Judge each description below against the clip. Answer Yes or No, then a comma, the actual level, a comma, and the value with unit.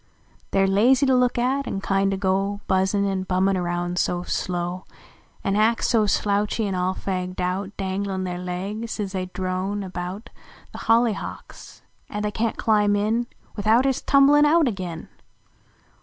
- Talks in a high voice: Yes, high, 195 Hz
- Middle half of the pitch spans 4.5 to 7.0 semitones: No, average, 3.0 semitones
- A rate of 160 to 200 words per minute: Yes, average, 170 wpm